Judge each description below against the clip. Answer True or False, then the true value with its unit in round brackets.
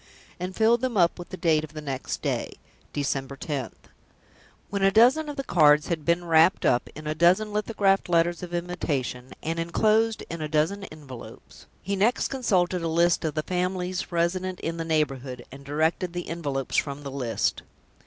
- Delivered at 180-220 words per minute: True (185 wpm)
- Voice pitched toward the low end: False (170 Hz)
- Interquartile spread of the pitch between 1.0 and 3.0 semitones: False (3.7 semitones)